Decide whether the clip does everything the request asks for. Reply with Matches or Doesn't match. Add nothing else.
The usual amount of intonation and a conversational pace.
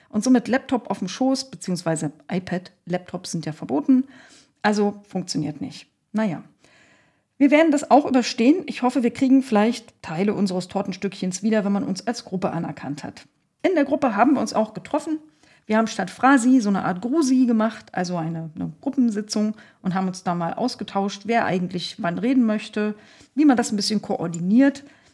Doesn't match